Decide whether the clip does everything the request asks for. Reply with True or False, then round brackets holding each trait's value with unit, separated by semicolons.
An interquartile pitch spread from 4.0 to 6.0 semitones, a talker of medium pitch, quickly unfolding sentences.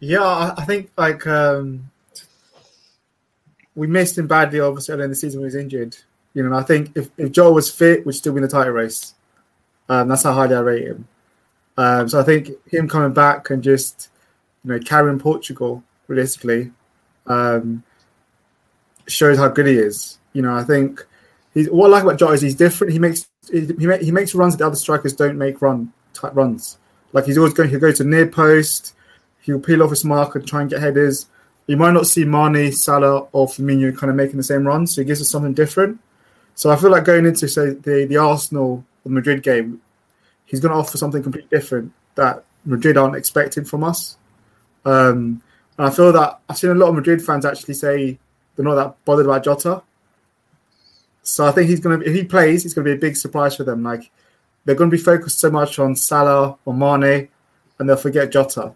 False (2.8 semitones; 145 Hz; 215 wpm)